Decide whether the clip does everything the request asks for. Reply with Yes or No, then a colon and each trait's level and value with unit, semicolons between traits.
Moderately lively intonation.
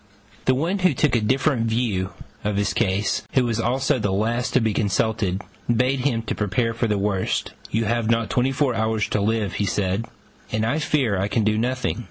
Yes: average, 3.4 semitones